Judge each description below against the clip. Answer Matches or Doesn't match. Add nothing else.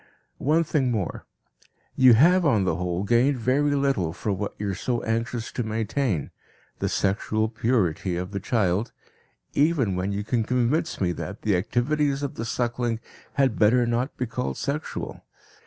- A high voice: Doesn't match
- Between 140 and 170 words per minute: Matches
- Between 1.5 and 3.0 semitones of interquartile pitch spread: Doesn't match